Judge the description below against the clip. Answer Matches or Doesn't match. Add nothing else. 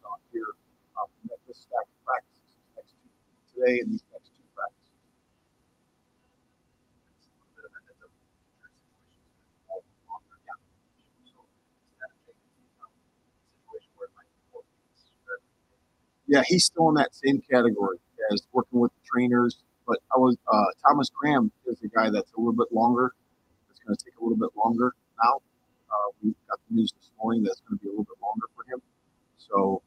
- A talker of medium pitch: Matches